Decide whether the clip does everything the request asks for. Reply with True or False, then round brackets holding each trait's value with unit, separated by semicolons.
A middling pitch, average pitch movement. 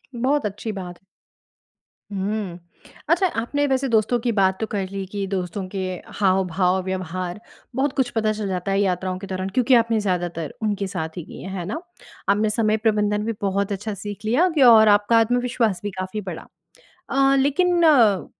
False (205 Hz; 3.6 semitones)